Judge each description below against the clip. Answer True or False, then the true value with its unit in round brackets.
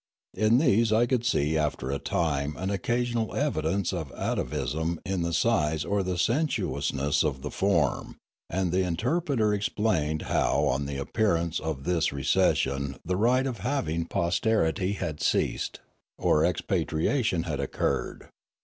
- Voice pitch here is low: True (90 Hz)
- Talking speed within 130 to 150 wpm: True (140 wpm)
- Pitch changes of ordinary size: False (6.2 semitones)